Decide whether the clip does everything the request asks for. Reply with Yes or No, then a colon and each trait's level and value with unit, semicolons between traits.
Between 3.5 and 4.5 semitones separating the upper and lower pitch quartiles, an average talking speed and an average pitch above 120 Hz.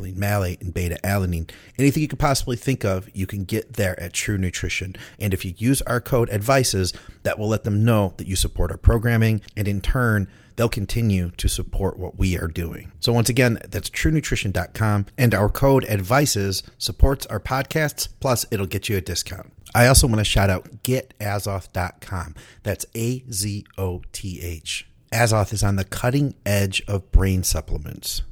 No: average, 3.9 semitones; average, 180 wpm; low, 105 Hz